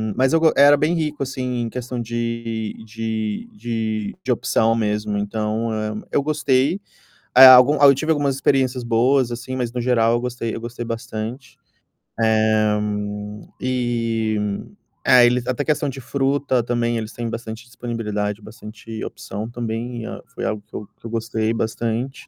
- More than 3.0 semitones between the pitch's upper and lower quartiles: No, narrow, 2.5 semitones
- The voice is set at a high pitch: No, low, 120 Hz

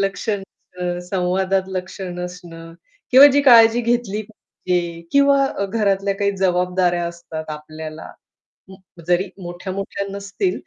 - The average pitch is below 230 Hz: Yes, high, 190 Hz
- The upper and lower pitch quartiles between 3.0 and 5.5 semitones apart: No, narrow, 2.5 semitones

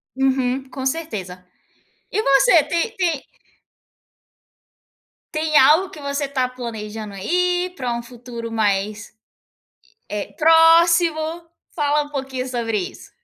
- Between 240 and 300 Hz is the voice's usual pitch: Yes, very high, 270 Hz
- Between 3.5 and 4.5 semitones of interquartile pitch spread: No, wide, 5.6 semitones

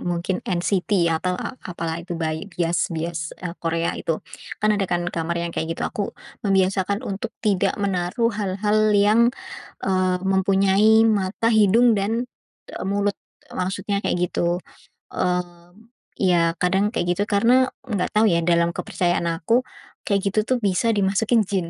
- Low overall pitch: No, high, 190 Hz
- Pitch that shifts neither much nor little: Yes, average, 3.2 semitones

